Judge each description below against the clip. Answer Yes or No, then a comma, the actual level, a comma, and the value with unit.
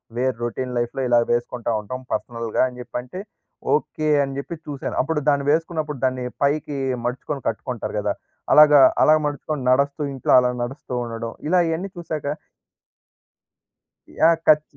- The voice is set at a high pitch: No, medium, 140 Hz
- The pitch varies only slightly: No, average, 3.5 semitones